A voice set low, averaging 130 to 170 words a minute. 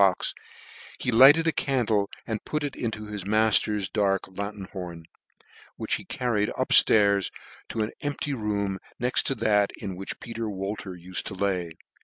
Yes: low, 105 Hz; average, 160 wpm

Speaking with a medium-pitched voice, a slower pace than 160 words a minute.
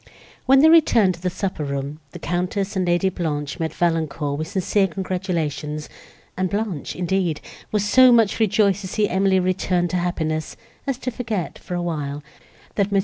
No: medium, 180 Hz; average, 175 wpm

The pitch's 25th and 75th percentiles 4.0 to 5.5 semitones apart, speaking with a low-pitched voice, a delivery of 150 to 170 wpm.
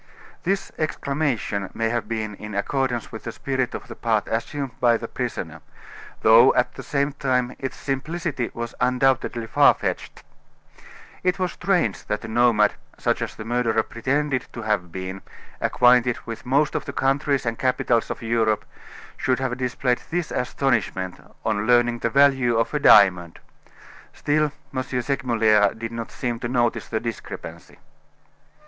No: average, 3.2 semitones; low, 120 Hz; average, 155 wpm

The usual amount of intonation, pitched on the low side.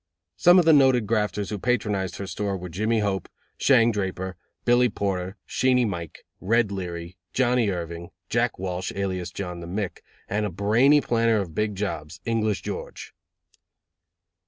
Yes: average, 4.0 semitones; low, 100 Hz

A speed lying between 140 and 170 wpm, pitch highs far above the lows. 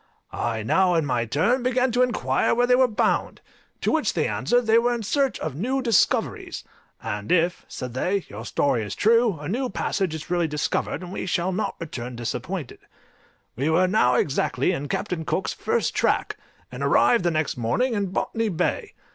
No: average, 190 wpm; wide, 8.9 semitones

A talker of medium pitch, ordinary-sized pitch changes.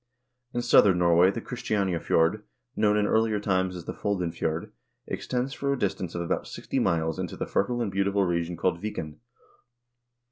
No: very low, 95 Hz; average, 3.8 semitones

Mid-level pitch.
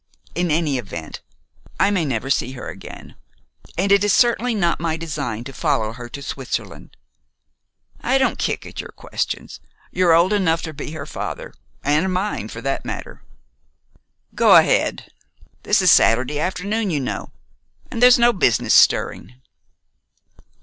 Yes: medium, 160 Hz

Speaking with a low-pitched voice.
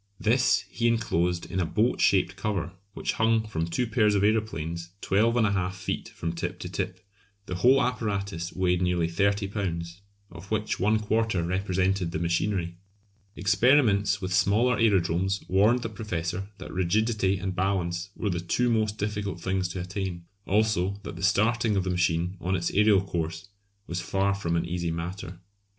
Yes: very low, 95 Hz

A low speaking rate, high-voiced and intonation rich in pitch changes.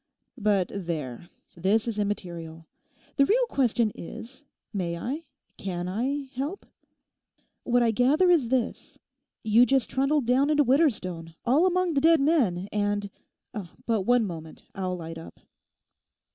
Yes: slow, 130 wpm; high, 230 Hz; wide, 7.0 semitones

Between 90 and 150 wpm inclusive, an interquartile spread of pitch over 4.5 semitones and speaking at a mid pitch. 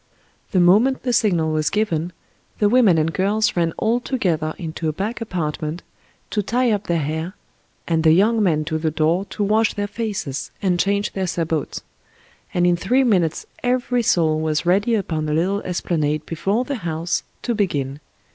No: average, 175 wpm; average, 5.0 semitones; medium, 180 Hz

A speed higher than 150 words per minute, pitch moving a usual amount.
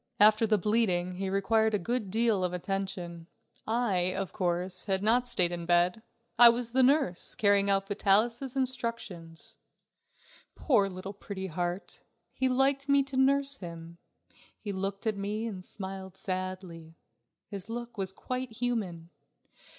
No: average, 145 wpm; average, 4.3 semitones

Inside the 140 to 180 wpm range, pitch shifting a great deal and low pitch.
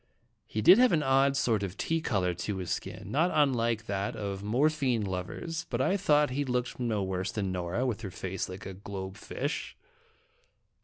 No: average, 190 wpm; wide, 6.2 semitones; low, 110 Hz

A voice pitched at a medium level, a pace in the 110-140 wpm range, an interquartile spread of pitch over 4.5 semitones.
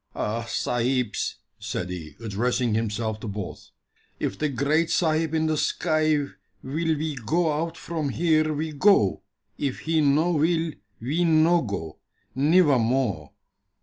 Yes: medium, 145 Hz; slow, 135 wpm; wide, 5.6 semitones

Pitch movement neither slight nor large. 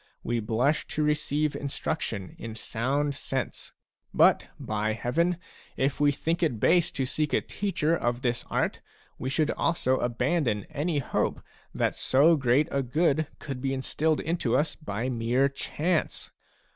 Yes: average, 4.1 semitones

